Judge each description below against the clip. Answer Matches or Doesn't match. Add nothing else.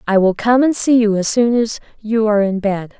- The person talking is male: Doesn't match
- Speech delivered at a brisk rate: Matches